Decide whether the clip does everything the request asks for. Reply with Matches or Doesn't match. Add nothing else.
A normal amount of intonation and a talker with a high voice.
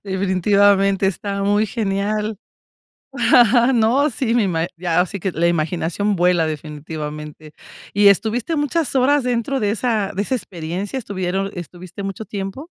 Matches